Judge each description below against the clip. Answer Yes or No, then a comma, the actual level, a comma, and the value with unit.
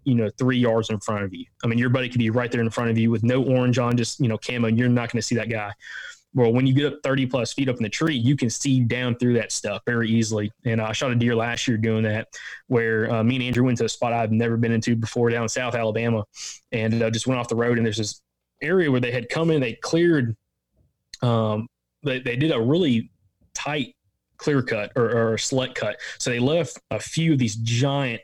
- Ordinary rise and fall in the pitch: No, narrow, 2.1 semitones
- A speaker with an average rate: No, fast, 265 wpm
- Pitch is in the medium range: No, low, 120 Hz